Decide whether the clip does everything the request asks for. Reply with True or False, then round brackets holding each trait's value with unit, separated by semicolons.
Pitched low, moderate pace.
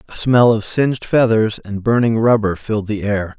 True (110 Hz; 195 wpm)